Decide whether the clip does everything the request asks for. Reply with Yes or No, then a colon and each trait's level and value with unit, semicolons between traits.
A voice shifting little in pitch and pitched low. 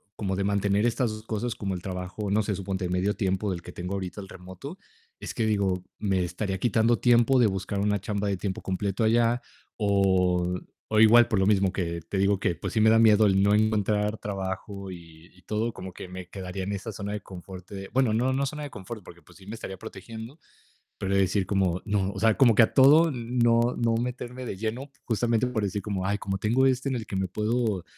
No: average, 3.1 semitones; low, 100 Hz